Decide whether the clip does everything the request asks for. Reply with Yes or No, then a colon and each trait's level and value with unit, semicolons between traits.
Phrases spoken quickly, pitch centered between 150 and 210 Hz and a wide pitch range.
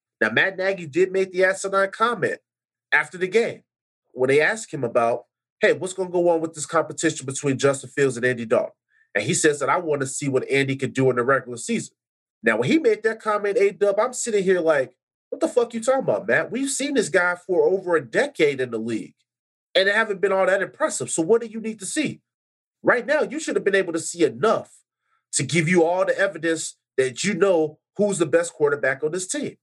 Yes: fast, 240 wpm; high, 190 Hz; wide, 7.4 semitones